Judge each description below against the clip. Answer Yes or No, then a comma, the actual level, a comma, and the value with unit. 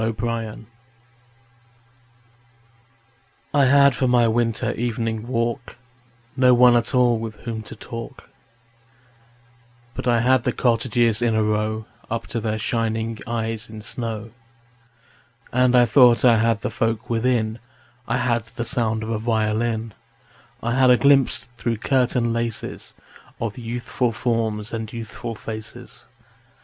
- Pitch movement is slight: Yes, narrow, 1.6 semitones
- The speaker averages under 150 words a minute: Yes, slow, 135 wpm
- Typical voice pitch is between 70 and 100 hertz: No, low, 115 Hz